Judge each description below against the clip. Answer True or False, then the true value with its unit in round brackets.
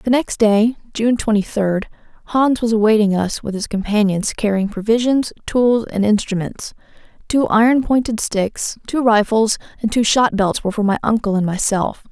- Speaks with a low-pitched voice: False (220 Hz)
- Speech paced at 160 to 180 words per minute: True (170 wpm)